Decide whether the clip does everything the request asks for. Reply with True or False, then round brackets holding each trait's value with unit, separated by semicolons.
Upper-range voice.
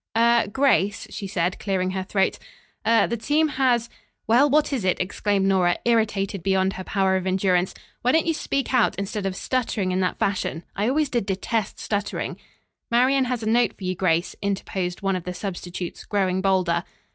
True (195 Hz)